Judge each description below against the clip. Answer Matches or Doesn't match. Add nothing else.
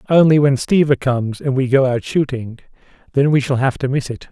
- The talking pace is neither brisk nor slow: Doesn't match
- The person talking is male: Matches